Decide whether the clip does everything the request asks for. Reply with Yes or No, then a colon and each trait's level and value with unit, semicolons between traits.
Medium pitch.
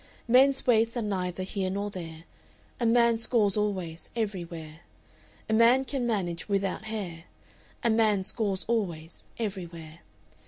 No: high, 205 Hz